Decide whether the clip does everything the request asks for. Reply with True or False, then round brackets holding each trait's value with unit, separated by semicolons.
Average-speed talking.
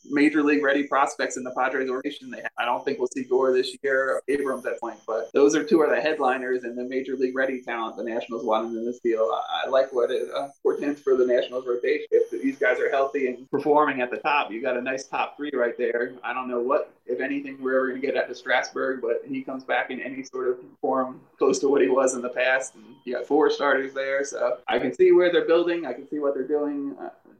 False (255 wpm)